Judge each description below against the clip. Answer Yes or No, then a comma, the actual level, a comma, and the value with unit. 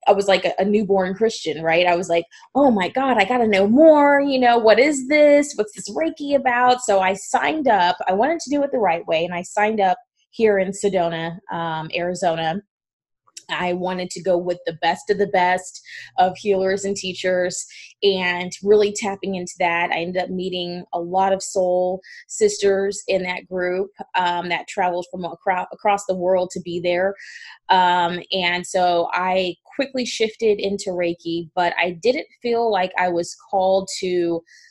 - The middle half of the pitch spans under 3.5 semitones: Yes, average, 3.0 semitones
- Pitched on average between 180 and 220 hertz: Yes, high, 190 Hz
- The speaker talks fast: No, average, 185 wpm